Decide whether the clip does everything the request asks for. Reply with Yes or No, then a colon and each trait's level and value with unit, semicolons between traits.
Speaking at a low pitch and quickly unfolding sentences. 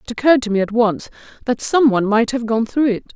No: high, 235 Hz; fast, 265 wpm